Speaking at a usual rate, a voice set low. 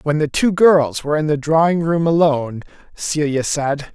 No: average, 185 wpm; medium, 150 Hz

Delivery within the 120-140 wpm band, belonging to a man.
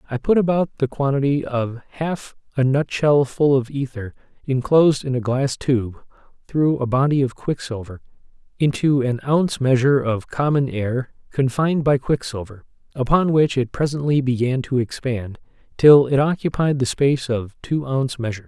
No: average, 160 wpm; male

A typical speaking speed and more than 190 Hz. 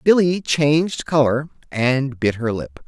No: average, 145 wpm; medium, 140 Hz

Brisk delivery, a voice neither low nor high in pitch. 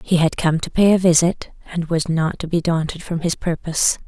Yes: fast, 235 wpm; medium, 170 Hz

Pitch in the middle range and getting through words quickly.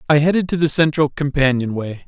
No: medium, 145 Hz; average, 175 wpm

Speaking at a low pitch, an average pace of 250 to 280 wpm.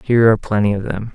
Yes: low, 105 Hz; fast, 260 wpm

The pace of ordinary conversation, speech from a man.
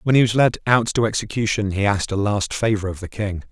No: fast, 255 wpm; male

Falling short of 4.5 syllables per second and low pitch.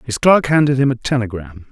No: 5.6 syllables/s; low, 125 Hz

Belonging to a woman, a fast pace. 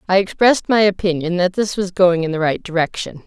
Yes: female; fast, 220 wpm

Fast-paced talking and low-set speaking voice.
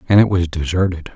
Yes: fast, 210 wpm; very low, 90 Hz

